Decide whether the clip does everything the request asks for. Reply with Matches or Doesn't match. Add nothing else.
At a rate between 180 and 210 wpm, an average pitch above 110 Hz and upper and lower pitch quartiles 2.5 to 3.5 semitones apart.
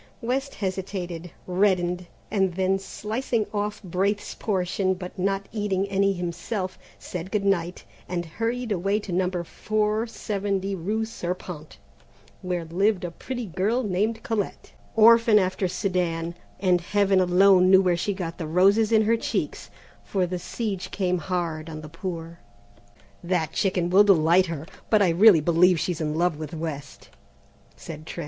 Doesn't match